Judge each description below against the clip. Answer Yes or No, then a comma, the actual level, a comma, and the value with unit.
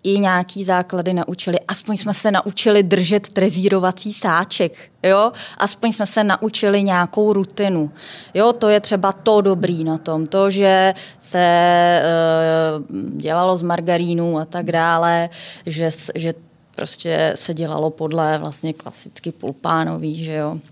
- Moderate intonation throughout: Yes, average, 3.4 semitones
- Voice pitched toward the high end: No, medium, 180 Hz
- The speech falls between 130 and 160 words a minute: Yes, average, 135 wpm